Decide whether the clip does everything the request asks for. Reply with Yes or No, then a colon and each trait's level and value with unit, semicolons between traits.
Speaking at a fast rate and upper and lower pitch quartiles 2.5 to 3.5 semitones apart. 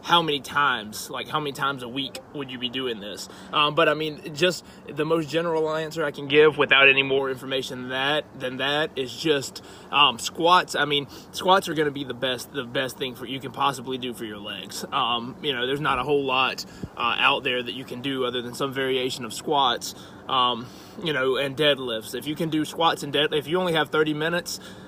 Yes: fast, 235 wpm; average, 3.2 semitones